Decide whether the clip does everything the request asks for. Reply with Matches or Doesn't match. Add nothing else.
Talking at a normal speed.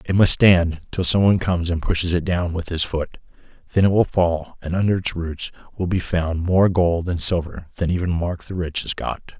Doesn't match